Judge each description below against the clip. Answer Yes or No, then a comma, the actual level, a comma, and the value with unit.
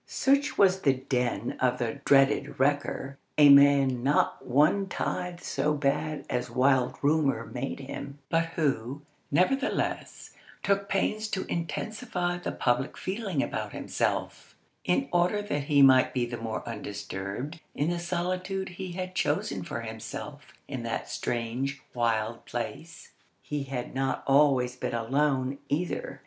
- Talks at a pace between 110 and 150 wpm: Yes, average, 140 wpm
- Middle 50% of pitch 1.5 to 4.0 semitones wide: No, wide, 5.4 semitones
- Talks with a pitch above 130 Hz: Yes, medium, 140 Hz